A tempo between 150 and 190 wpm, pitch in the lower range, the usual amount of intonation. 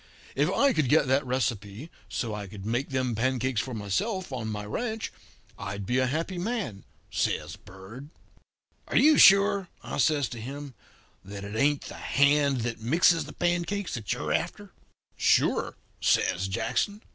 No: average, 160 wpm; low, 130 Hz; wide, 7.3 semitones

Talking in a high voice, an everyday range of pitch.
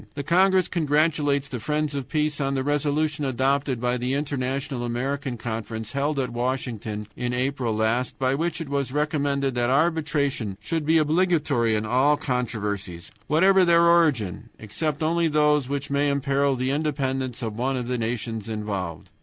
No: low, 135 Hz; average, 3.6 semitones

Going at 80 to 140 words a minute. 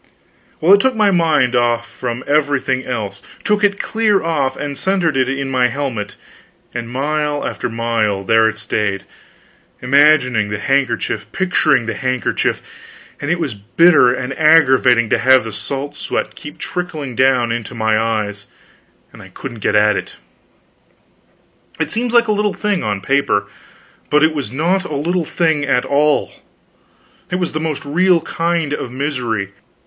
No: average, 160 wpm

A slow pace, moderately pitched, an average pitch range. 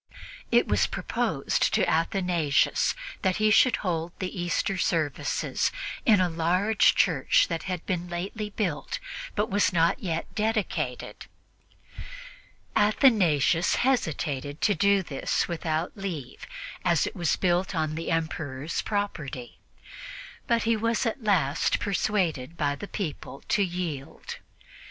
Yes: slow, 125 wpm; medium, 175 Hz; average, 4.2 semitones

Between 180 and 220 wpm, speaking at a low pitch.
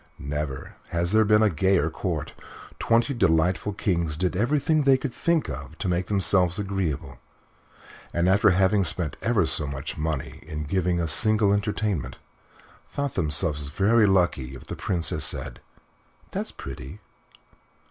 No: average, 145 wpm; very low, 90 Hz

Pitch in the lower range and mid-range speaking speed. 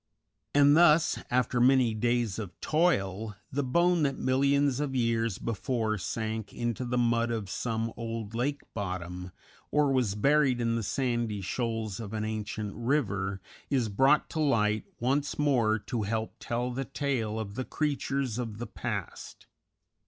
Yes: low, 115 Hz; average, 150 wpm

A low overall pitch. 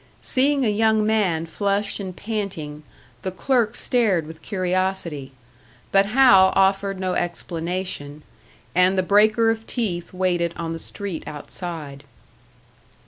No: high, 190 Hz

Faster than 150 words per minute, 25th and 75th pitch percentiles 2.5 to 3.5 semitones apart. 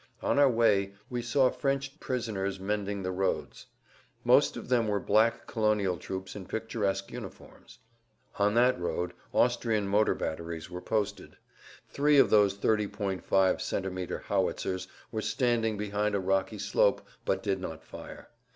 No: average, 140 wpm; average, 3.2 semitones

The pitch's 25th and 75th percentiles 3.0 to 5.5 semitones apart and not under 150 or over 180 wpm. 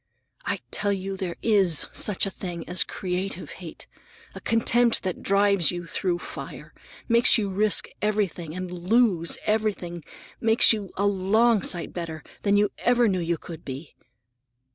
Yes: average, 3.3 semitones; average, 155 wpm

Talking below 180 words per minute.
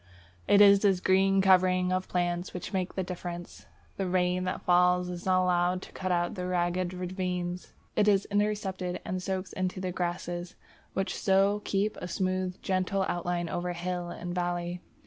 Yes: average, 165 wpm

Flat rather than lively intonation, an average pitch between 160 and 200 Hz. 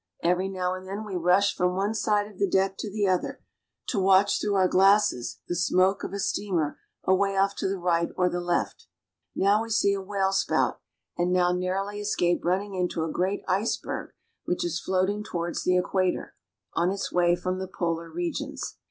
Yes: narrow, 1.9 semitones; medium, 185 Hz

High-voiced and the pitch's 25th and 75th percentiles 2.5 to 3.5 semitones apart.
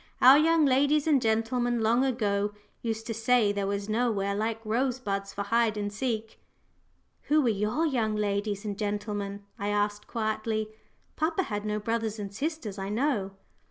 Yes: high, 220 Hz; average, 3.1 semitones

